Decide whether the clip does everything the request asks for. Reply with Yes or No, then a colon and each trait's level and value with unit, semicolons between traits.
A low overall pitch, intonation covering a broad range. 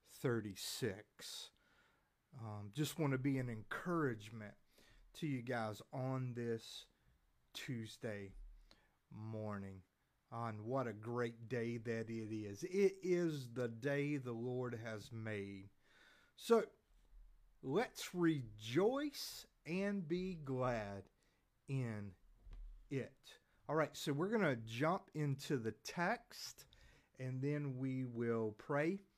No: low, 125 Hz; average, 5.0 semitones